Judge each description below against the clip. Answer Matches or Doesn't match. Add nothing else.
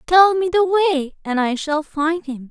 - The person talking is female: Matches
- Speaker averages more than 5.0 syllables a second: Doesn't match